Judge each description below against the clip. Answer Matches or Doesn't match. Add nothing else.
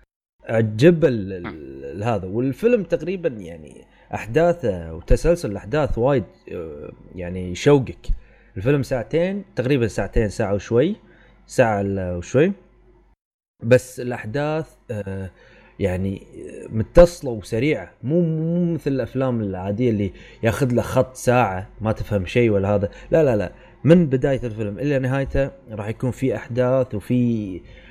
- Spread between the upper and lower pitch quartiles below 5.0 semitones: Doesn't match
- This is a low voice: Matches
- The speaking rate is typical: Matches